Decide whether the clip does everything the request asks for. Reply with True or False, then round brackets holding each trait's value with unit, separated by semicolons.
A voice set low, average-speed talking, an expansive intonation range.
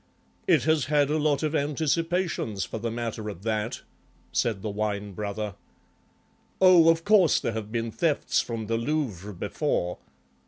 True (115 Hz; 155 wpm; 6.6 semitones)